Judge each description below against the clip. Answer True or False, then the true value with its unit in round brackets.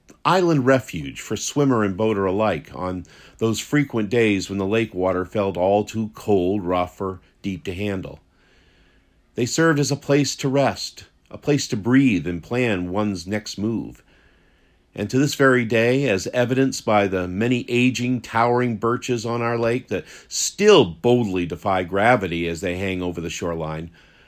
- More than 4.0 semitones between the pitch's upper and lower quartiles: True (5.2 semitones)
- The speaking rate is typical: True (165 wpm)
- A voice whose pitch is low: True (105 Hz)